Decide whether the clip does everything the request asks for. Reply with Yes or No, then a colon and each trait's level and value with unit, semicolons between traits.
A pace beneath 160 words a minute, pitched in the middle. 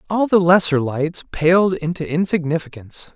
Yes: slow, 135 wpm; medium, 165 Hz